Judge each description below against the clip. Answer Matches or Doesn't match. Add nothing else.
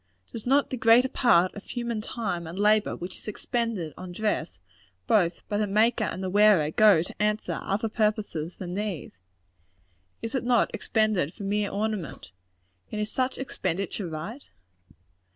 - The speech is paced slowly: Doesn't match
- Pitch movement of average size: Matches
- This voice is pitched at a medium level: Doesn't match